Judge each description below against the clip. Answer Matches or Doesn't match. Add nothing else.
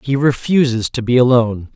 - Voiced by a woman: Doesn't match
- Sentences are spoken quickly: Doesn't match